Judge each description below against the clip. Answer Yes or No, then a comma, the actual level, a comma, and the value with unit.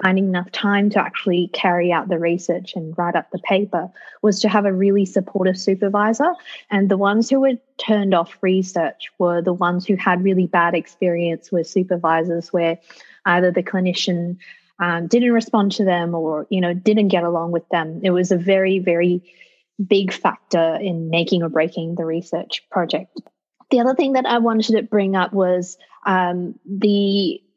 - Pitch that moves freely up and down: No, average, 2.7 semitones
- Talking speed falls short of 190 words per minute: Yes, average, 180 wpm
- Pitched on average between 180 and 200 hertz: Yes, medium, 185 Hz